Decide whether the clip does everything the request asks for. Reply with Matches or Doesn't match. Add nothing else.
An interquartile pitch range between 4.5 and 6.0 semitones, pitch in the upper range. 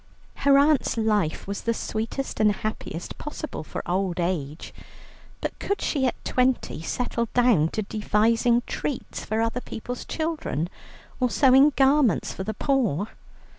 Matches